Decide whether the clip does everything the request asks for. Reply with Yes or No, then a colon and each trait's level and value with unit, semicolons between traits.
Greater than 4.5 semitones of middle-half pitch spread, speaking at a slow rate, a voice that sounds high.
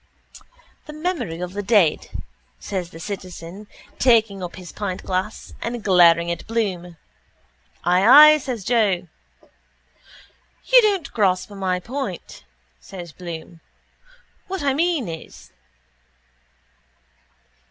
Yes: wide, 5.4 semitones; slow, 105 wpm; high, 195 Hz